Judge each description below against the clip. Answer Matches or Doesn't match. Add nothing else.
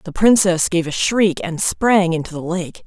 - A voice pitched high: Doesn't match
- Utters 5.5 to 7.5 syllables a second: Doesn't match